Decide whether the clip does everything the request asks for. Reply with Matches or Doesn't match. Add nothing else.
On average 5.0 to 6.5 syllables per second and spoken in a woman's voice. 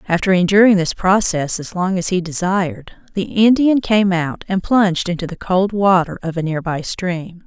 Doesn't match